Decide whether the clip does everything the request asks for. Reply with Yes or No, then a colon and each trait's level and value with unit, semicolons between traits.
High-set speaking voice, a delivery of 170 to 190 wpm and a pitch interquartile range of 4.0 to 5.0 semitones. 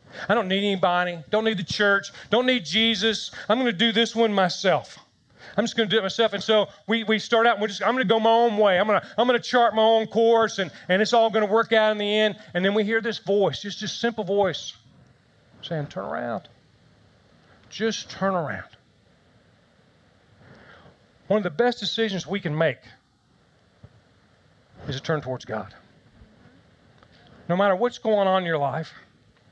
No: high, 205 Hz; average, 200 wpm; average, 4.3 semitones